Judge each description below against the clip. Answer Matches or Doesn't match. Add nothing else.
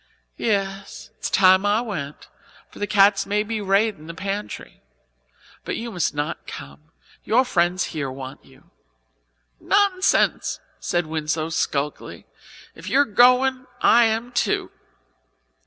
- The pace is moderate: Doesn't match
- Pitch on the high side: Matches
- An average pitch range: Doesn't match